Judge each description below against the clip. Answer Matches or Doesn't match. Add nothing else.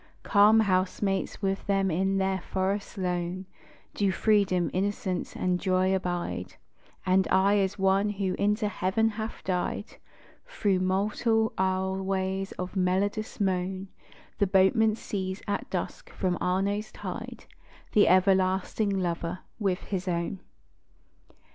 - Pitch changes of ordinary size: Doesn't match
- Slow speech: Matches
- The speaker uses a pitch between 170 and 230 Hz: Matches